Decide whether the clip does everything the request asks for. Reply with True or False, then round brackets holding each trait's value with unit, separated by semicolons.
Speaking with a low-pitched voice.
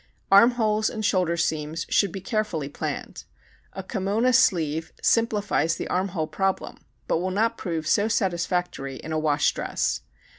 False (185 Hz)